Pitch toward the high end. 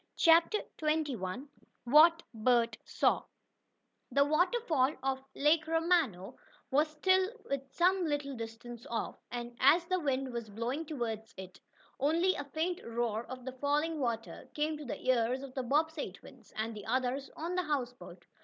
Yes: very high, 275 Hz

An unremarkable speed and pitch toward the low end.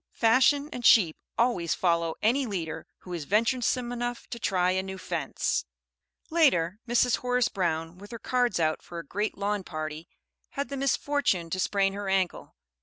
No: average, 170 wpm; high, 200 Hz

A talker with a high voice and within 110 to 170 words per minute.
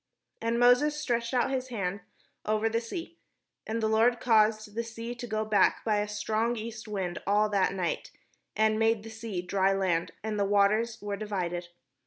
No: high, 215 Hz; average, 185 wpm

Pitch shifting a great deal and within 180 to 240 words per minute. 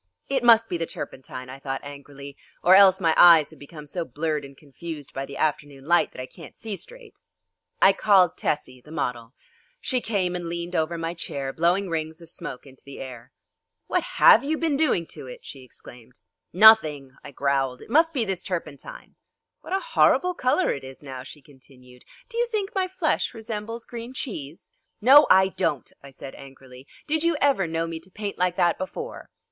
Yes: wide, 7.9 semitones; average, 195 wpm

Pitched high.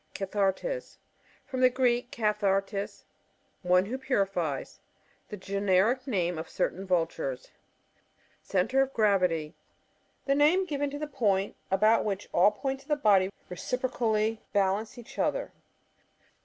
Yes: high, 210 Hz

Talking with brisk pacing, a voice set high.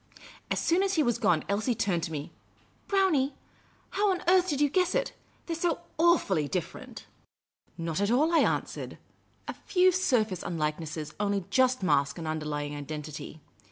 No: average, 180 wpm; high, 205 Hz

